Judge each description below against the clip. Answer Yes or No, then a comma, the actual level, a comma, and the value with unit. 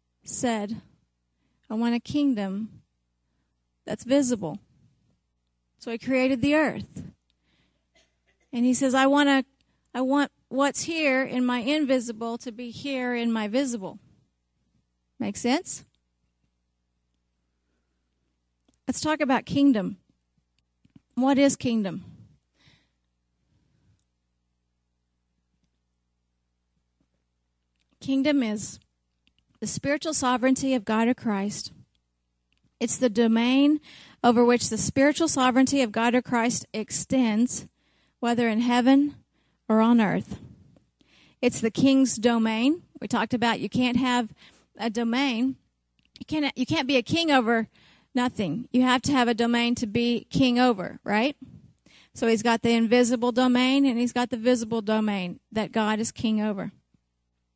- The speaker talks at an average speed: No, slow, 120 wpm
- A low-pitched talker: No, high, 235 Hz